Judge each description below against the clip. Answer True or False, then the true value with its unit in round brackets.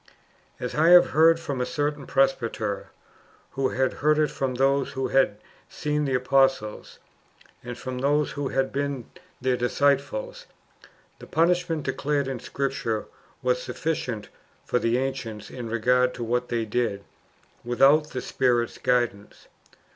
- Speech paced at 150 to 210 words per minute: False (140 wpm)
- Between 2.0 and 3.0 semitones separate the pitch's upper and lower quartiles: True (2.7 semitones)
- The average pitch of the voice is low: True (130 Hz)